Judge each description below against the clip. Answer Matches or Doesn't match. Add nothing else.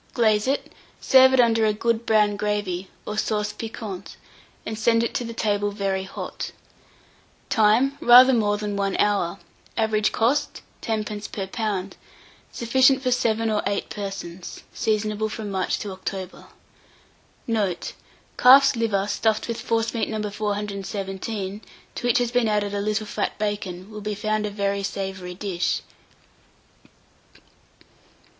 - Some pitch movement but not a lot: Doesn't match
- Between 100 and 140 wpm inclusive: Matches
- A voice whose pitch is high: Matches